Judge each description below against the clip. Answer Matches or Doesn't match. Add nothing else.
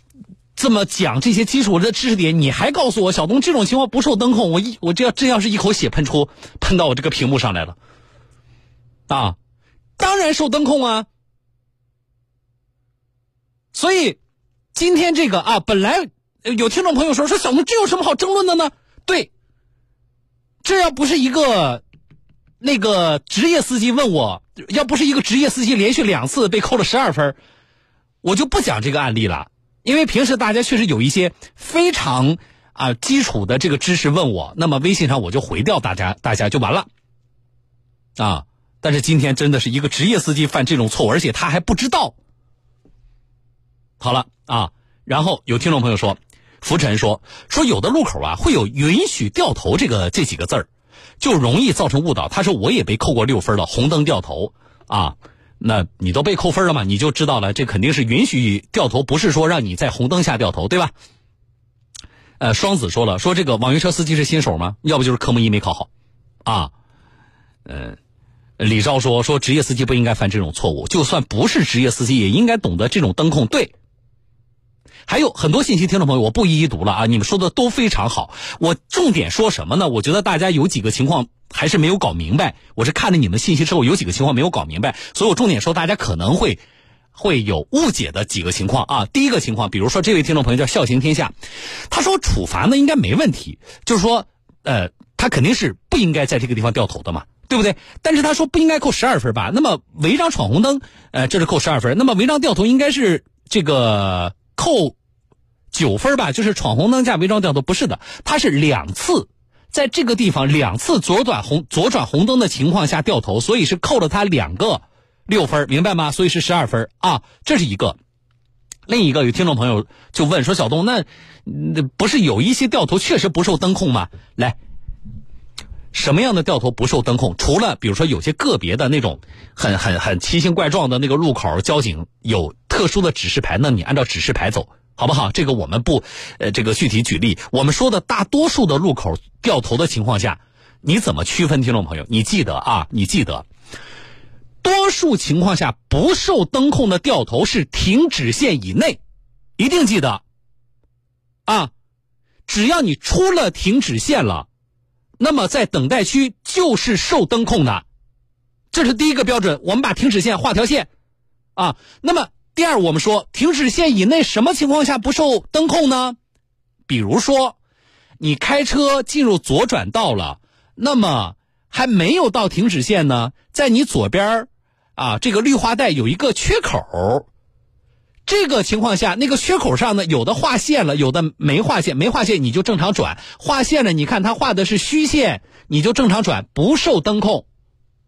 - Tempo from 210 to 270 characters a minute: Doesn't match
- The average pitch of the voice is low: Doesn't match